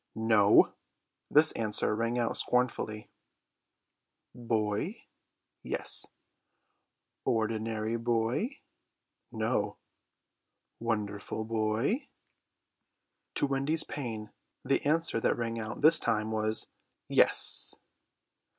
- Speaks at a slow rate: Yes, slow, 80 wpm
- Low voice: Yes, low, 115 Hz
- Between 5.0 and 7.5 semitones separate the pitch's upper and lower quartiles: No, narrow, 2.5 semitones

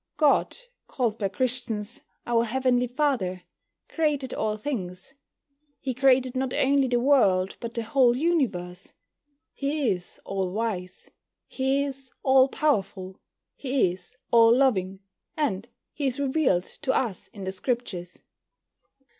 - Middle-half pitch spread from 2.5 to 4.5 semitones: No, wide, 5.6 semitones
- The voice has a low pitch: No, high, 245 Hz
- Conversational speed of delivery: No, slow, 130 wpm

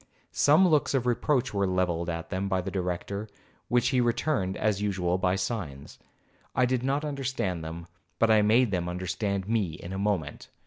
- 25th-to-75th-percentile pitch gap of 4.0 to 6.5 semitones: Yes, average, 5.1 semitones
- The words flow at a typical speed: Yes, average, 180 wpm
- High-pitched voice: No, low, 100 Hz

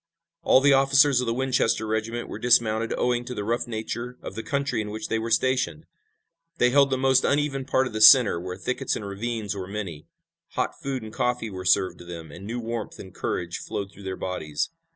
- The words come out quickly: Yes, fast, 215 wpm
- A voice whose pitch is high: No, low, 115 Hz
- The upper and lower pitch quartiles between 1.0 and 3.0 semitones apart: No, average, 4.3 semitones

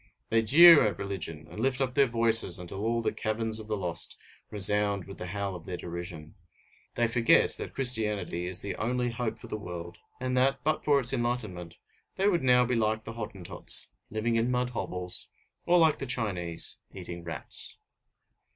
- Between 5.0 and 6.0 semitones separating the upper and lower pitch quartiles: Yes, average, 5.3 semitones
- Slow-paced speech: No, average, 185 wpm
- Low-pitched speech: Yes, low, 110 Hz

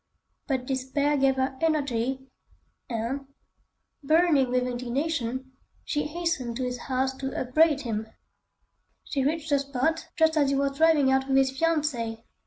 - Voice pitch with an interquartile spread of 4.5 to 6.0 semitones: No, average, 2.8 semitones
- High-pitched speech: Yes, very high, 270 Hz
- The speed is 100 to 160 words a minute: Yes, average, 145 wpm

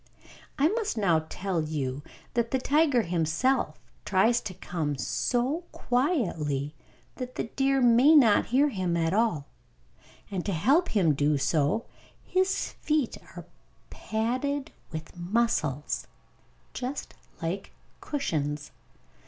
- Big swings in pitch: Yes, wide, 8.9 semitones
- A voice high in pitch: Yes, high, 215 Hz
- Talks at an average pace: No, slow, 120 wpm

